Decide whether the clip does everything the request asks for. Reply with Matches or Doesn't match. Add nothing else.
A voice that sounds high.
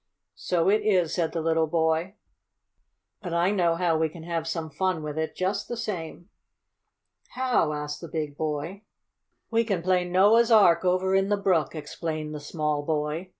Doesn't match